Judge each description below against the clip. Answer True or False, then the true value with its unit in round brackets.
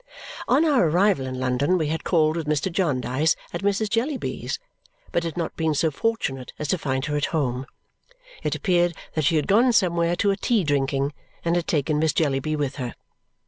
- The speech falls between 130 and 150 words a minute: False (195 wpm)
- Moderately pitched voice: True (160 Hz)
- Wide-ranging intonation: False (4.5 semitones)